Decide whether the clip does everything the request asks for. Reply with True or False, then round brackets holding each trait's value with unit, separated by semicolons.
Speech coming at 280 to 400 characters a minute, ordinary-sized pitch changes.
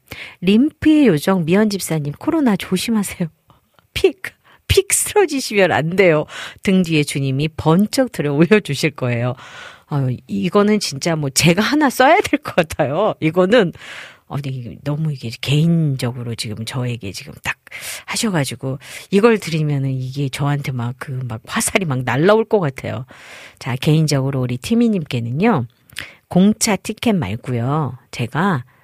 False (295 characters per minute; 7.7 semitones)